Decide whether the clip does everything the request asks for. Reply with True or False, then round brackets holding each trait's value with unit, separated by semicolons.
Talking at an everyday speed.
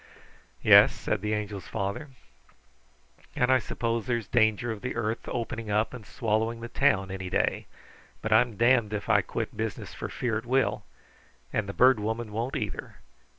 True (170 wpm)